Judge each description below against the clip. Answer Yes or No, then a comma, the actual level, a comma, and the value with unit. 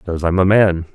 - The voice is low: Yes, very low, 90 Hz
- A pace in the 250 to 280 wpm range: Yes, fast, 255 wpm